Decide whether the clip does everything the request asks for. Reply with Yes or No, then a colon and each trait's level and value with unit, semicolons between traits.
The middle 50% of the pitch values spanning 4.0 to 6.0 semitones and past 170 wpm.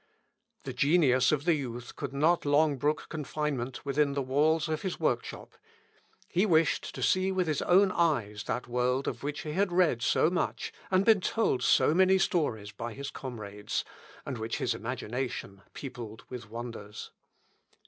No: average, 5.2 semitones; average, 165 wpm